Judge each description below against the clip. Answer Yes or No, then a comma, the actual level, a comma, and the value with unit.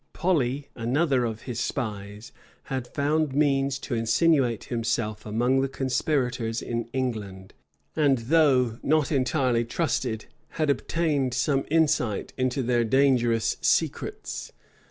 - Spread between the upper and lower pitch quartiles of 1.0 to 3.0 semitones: No, average, 3.4 semitones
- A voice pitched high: No, low, 130 Hz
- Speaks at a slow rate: Yes, slow, 115 wpm